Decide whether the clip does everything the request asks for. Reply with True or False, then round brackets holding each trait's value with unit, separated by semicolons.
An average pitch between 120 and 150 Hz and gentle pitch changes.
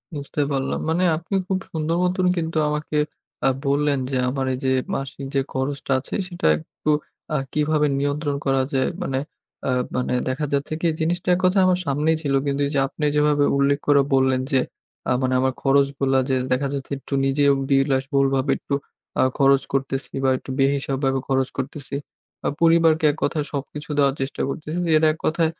True (140 Hz; 2.3 semitones)